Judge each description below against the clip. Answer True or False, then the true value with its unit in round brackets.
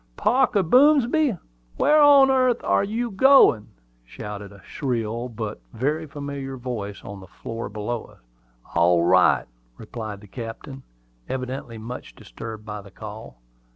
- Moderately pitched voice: False (120 Hz)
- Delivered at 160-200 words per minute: False (135 wpm)